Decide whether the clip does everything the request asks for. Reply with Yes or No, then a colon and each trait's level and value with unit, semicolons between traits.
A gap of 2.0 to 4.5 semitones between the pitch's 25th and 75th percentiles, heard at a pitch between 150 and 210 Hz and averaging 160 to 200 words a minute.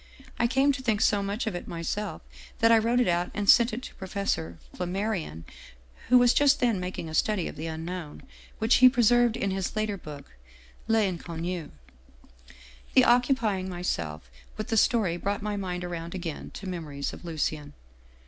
No: average, 5.2 semitones; high, 190 Hz; average, 175 wpm